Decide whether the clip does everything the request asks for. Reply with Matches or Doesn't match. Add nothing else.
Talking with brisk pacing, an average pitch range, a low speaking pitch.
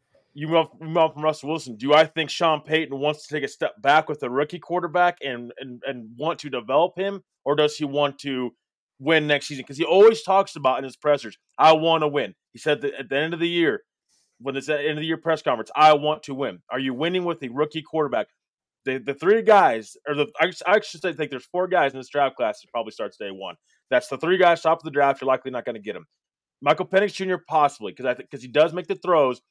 Doesn't match